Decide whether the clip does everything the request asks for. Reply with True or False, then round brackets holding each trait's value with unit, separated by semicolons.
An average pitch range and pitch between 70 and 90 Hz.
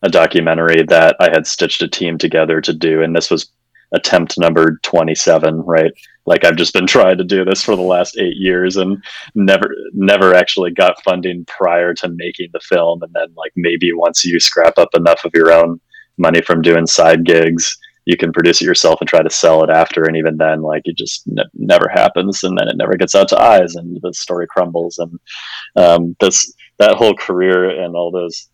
False (1.6 semitones; 85 Hz)